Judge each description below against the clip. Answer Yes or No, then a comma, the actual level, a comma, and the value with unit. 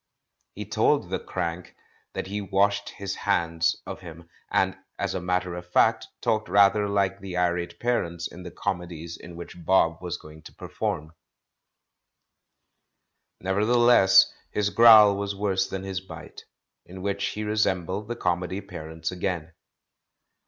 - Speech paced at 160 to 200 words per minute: No, average, 150 wpm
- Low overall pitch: Yes, very low, 95 Hz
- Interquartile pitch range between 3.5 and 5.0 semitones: No, average, 2.7 semitones